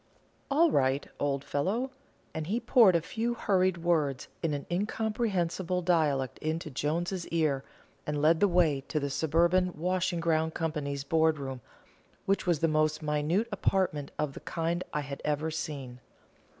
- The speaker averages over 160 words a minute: No, average, 155 wpm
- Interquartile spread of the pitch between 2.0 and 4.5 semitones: Yes, average, 3.8 semitones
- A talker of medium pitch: Yes, medium, 160 Hz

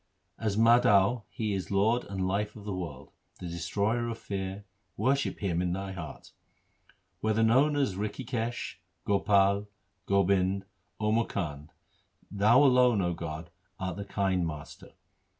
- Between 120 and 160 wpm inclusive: Yes, average, 140 wpm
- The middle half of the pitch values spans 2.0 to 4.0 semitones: Yes, average, 3.3 semitones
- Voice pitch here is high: No, low, 100 Hz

